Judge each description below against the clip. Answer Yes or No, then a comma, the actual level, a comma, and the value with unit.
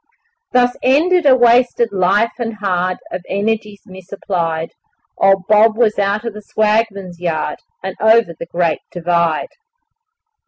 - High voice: Yes, high, 205 Hz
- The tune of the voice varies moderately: Yes, average, 4.2 semitones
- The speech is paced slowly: Yes, slow, 130 wpm